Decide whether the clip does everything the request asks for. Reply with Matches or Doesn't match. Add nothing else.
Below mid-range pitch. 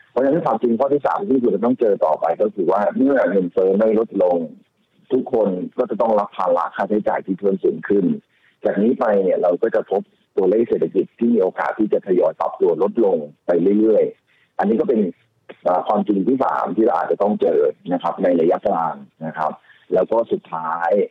Doesn't match